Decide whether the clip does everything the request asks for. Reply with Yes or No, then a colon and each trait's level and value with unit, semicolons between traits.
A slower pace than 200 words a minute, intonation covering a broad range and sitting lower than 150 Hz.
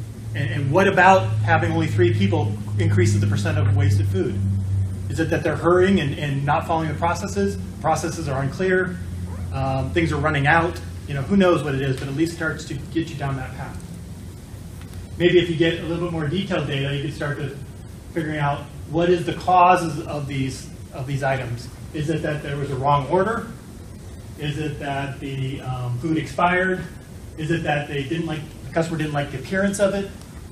No: fast, 205 wpm; wide, 7.1 semitones; medium, 140 Hz